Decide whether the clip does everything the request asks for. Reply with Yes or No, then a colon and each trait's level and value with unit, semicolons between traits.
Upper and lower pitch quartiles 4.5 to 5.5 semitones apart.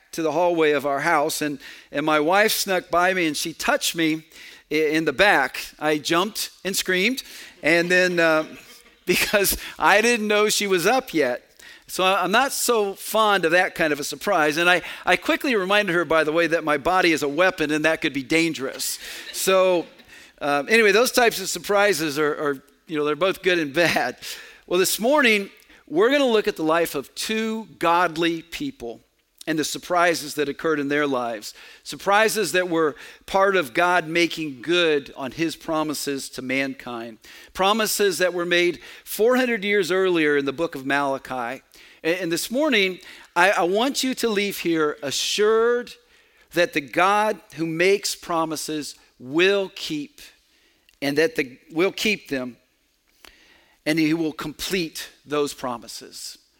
Yes: average, 5.1 semitones